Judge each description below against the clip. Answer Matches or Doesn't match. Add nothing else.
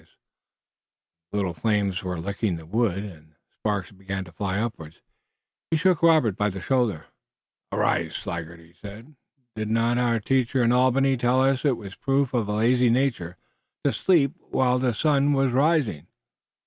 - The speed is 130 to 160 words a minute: Doesn't match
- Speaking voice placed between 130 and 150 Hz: Doesn't match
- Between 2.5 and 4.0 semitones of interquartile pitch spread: Doesn't match